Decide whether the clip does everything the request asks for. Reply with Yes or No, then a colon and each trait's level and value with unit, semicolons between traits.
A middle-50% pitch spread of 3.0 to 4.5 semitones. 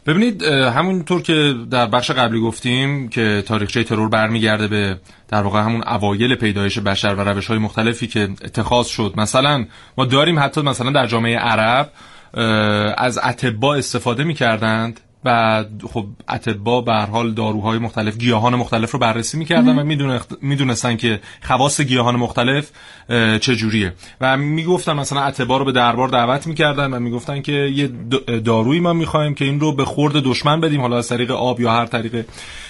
Yes: average, 3.7 semitones